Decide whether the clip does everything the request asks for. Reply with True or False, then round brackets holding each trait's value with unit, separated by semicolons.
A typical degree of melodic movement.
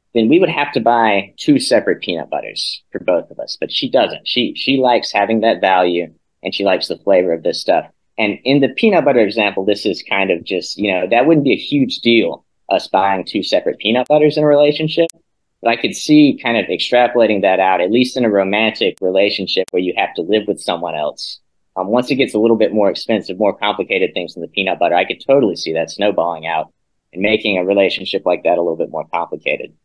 False (7.2 semitones)